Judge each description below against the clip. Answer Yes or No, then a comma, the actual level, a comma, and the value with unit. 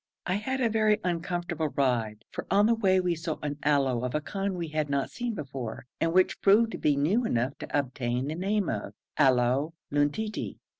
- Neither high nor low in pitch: Yes, medium, 160 Hz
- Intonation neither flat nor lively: No, wide, 6.2 semitones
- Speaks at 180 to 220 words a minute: Yes, average, 200 wpm